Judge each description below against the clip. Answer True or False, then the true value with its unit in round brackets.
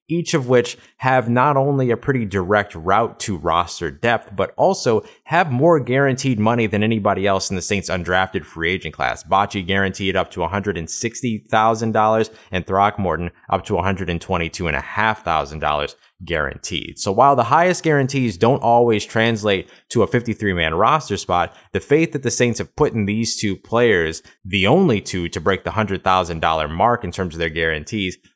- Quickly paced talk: False (165 wpm)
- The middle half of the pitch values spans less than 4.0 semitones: False (4.4 semitones)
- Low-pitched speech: True (105 Hz)